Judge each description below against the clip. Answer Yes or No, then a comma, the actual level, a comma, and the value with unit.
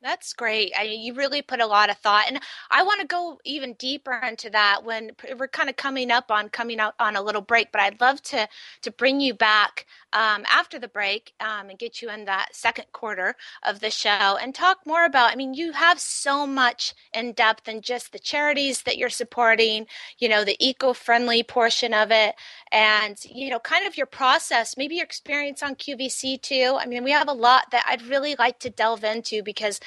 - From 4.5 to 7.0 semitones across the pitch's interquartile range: No, average, 3.8 semitones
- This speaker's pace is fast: Yes, fast, 220 wpm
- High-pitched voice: Yes, high, 240 Hz